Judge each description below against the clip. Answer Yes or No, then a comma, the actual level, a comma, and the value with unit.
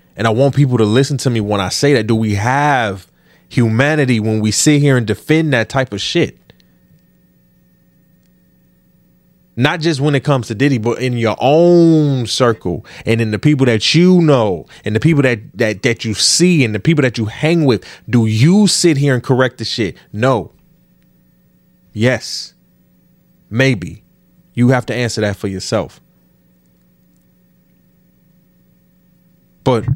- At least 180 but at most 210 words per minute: No, average, 160 wpm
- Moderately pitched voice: No, low, 120 Hz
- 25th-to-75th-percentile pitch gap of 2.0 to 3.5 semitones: No, average, 5.0 semitones